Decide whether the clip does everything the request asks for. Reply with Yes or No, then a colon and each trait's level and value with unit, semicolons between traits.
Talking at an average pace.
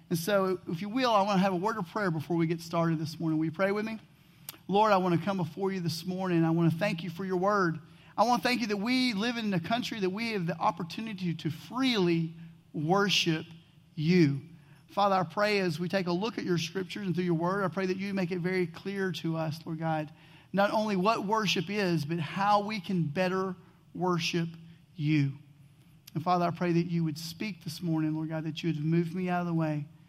No: fast, 240 wpm